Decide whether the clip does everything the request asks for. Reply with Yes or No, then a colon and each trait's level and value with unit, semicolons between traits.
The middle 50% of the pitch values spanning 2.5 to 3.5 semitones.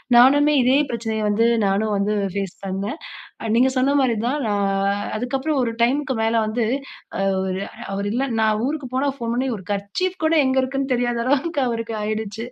No: average, 4.2 semitones